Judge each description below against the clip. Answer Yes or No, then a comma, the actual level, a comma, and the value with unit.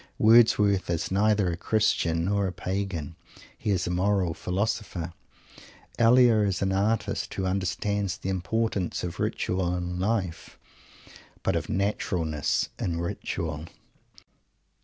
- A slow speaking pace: Yes, slow, 120 wpm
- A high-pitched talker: No, very low, 95 Hz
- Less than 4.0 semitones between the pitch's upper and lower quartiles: Yes, average, 2.8 semitones